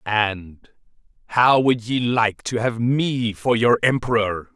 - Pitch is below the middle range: Yes, low, 115 Hz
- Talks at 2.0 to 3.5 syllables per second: Yes, 3.4 syllables/s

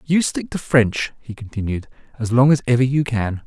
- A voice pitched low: Yes, low, 120 Hz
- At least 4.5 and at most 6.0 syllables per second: Yes, 5.1 syllables/s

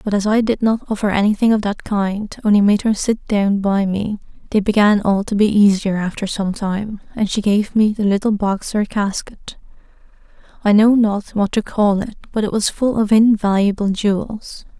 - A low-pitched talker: No, high, 205 Hz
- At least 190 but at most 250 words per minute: Yes, average, 200 wpm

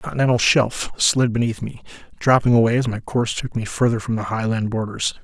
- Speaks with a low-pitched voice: Yes, low, 115 Hz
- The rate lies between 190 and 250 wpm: Yes, fast, 205 wpm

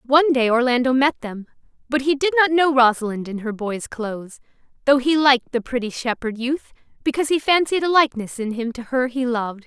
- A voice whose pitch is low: No, very high, 255 Hz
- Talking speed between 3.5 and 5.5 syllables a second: No, 5.8 syllables/s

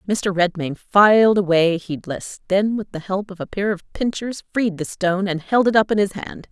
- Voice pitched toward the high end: Yes, high, 195 Hz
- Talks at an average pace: No, fast, 220 wpm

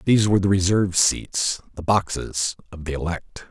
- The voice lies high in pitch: No, very low, 90 Hz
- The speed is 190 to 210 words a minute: No, average, 170 wpm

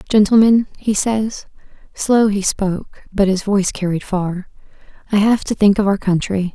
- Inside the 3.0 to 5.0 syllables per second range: Yes, 4.8 syllables/s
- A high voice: Yes, high, 200 Hz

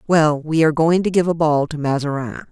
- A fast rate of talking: Yes, fast, 240 wpm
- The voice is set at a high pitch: No, medium, 155 Hz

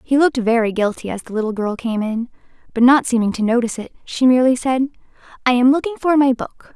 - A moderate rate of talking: No, fast, 220 wpm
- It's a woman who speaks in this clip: Yes, female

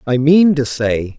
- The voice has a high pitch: No, medium, 140 Hz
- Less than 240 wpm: Yes, average, 200 wpm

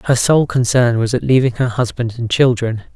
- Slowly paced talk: No, fast, 205 wpm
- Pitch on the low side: Yes, low, 120 Hz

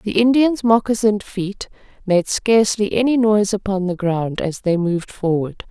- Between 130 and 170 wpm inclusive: Yes, average, 160 wpm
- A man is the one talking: No, female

